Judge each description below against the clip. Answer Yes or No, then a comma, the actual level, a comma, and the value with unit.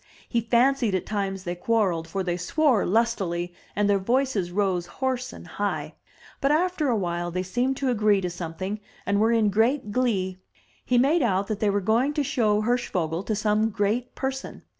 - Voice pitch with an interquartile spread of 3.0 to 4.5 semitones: No, average, 4.9 semitones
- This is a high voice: Yes, high, 210 Hz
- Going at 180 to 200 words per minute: Yes, average, 185 wpm